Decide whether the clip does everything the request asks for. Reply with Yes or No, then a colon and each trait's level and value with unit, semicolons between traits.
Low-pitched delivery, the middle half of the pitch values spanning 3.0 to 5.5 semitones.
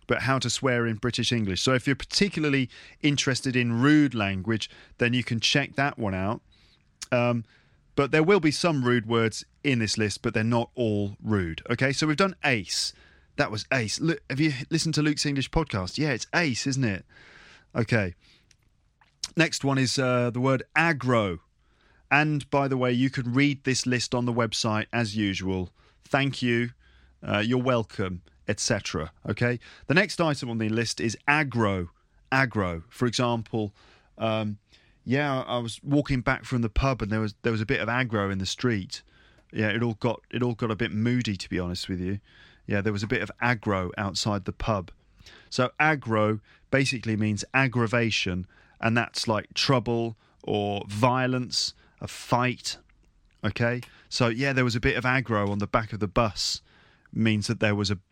Yes: low, 120 Hz; average, 3.9 semitones